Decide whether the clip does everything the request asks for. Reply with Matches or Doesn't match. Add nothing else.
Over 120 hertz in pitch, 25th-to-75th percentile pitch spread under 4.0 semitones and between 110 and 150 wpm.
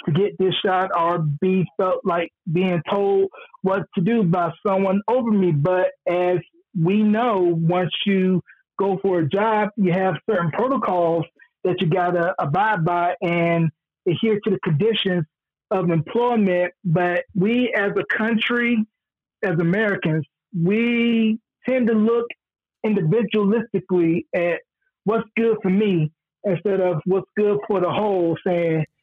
Matches